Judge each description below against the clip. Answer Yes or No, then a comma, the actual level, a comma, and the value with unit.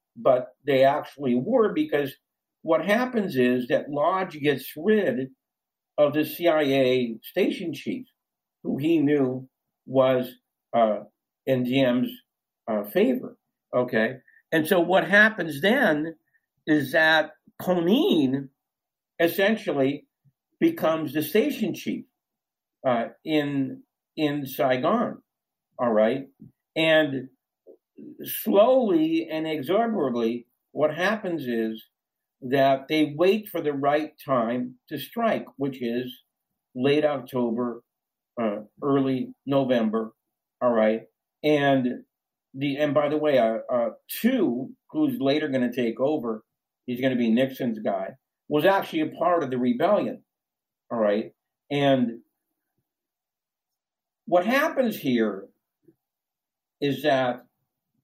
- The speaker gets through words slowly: Yes, slow, 110 wpm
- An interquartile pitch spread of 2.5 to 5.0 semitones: No, wide, 5.4 semitones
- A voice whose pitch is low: No, medium, 145 Hz